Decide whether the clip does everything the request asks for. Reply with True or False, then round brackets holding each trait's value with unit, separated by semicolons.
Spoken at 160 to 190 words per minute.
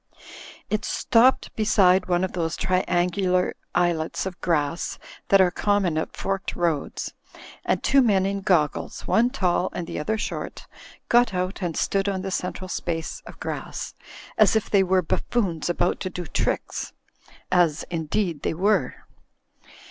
False (150 wpm)